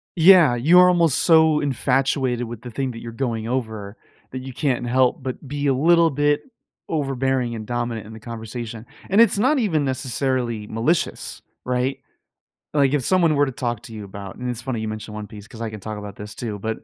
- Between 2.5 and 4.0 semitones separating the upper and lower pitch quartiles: No, average, 4.4 semitones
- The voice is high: No, low, 125 Hz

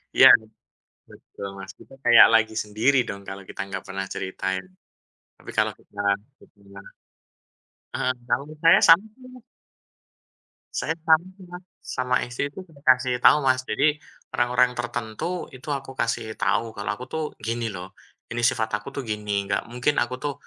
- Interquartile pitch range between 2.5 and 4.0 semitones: No, average, 4.6 semitones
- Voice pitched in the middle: No, low, 120 Hz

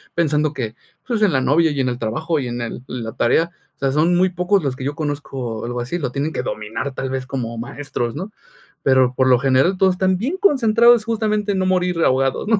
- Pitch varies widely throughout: Yes, wide, 6.3 semitones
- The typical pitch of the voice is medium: Yes, medium, 145 Hz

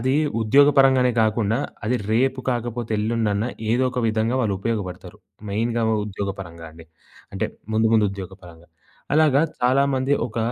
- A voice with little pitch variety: No, average, 3.9 semitones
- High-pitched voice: No, low, 115 Hz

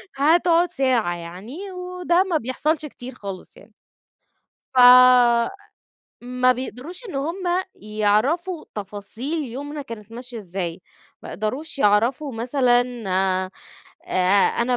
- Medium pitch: No, very high, 250 Hz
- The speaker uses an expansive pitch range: Yes, wide, 6.5 semitones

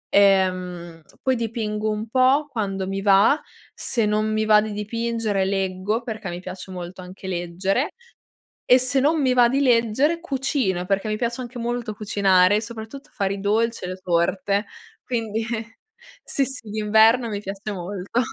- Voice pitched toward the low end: No, high, 215 Hz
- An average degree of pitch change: Yes, average, 3.6 semitones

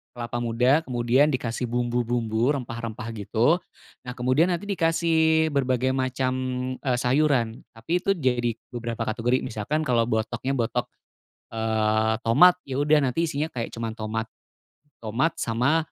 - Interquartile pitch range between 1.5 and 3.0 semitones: No, average, 4.1 semitones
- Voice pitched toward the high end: No, low, 125 Hz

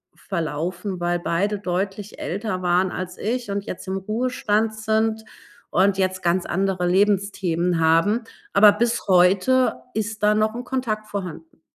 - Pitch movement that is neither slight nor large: Yes, average, 3.1 semitones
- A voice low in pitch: No, high, 195 Hz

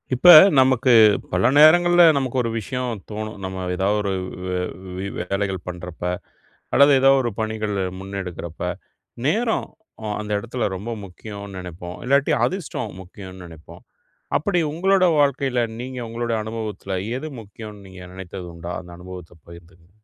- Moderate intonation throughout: No, wide, 5.8 semitones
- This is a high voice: No, low, 105 Hz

